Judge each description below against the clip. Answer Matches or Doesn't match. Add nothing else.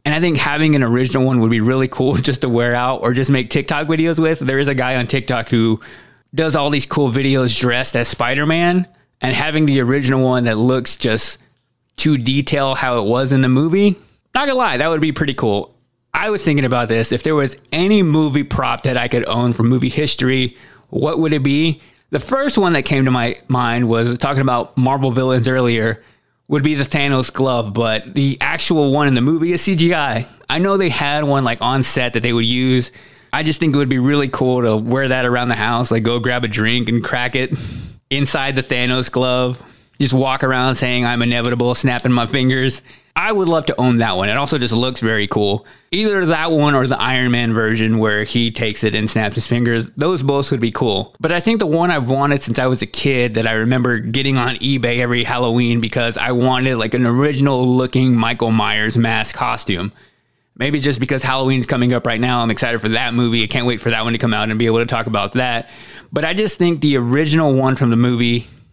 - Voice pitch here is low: Matches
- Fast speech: Matches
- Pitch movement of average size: Matches